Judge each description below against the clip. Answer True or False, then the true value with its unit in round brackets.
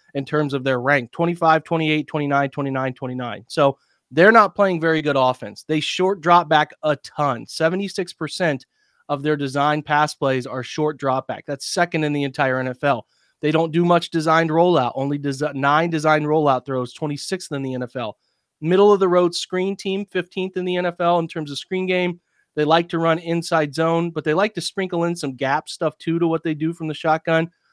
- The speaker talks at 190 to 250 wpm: True (200 wpm)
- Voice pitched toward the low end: False (155 Hz)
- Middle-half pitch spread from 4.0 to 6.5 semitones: False (3.3 semitones)